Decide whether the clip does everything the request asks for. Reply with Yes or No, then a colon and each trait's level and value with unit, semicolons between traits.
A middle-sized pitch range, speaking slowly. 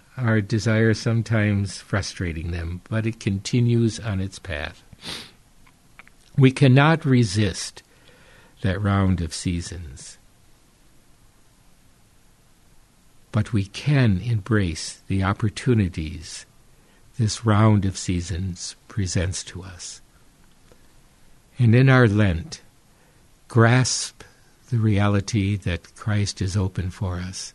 Yes: average, 3.5 semitones; slow, 95 wpm